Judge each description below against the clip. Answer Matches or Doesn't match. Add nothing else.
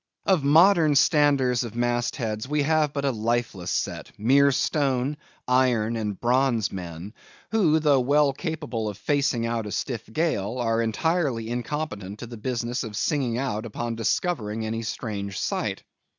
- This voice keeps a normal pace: Matches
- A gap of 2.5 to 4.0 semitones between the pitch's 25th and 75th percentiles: Doesn't match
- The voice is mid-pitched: Doesn't match